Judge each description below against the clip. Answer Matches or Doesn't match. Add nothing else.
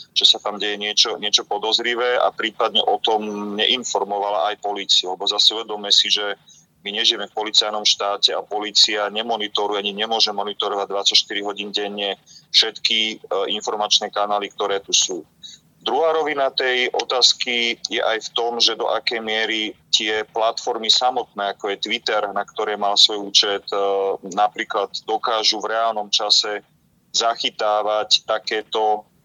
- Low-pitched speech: Matches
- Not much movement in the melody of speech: Matches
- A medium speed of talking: Matches